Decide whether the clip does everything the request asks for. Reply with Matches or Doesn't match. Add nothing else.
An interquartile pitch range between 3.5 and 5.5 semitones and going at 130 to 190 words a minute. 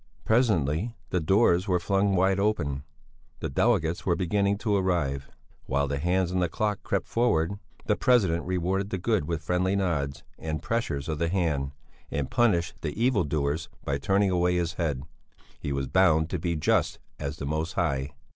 Matches